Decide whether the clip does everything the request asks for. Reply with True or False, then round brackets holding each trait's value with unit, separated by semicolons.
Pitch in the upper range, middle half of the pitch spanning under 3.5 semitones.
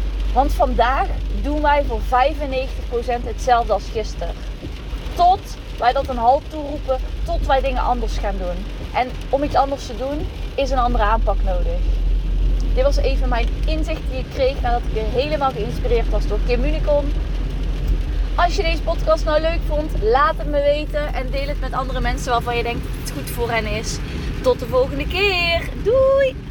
False (275 Hz; 5.1 semitones)